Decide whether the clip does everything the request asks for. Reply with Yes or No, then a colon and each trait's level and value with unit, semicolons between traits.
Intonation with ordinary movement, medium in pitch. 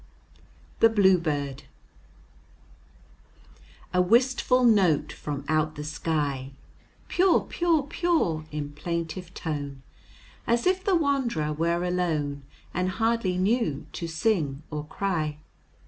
No: wide, 7.2 semitones; medium, 170 Hz